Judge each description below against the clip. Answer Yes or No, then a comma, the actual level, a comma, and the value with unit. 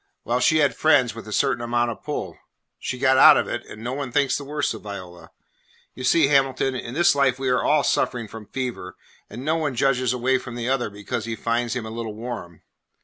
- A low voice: Yes, low, 125 Hz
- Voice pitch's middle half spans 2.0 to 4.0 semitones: Yes, average, 2.9 semitones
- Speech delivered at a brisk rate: Yes, fast, 230 wpm